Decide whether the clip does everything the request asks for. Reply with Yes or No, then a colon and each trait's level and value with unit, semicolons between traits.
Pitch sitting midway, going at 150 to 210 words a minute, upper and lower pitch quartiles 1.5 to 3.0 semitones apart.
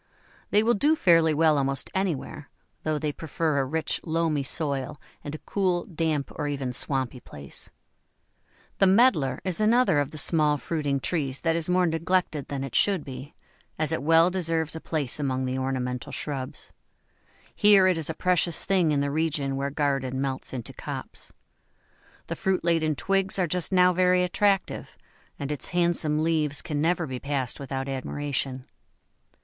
No: medium, 155 Hz; average, 165 wpm; average, 4.2 semitones